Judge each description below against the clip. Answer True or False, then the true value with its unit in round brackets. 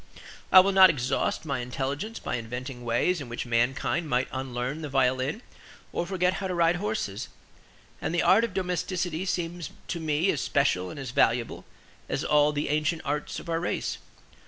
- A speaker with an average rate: True (180 wpm)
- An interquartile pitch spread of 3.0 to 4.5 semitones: False (5.5 semitones)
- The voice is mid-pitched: True (150 Hz)